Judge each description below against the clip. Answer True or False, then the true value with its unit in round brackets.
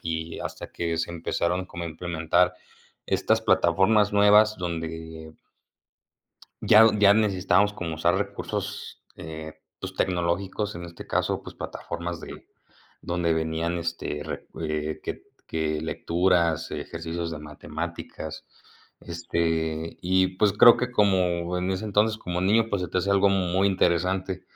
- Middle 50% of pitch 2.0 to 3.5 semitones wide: True (2.7 semitones)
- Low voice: True (85 Hz)